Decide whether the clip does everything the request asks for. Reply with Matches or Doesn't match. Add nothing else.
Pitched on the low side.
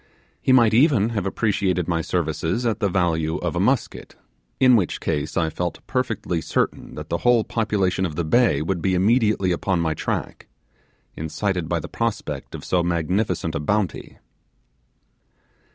Matches